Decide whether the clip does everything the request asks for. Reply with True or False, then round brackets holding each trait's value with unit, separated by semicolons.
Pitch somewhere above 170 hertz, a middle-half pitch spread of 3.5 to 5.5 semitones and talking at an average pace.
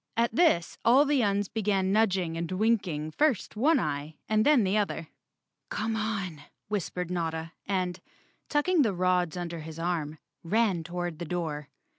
True (185 Hz; 4.8 semitones; 155 wpm)